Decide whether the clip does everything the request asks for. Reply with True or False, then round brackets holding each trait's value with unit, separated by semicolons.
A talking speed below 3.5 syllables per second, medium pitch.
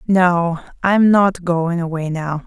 True (3.3 syllables/s; 175 Hz)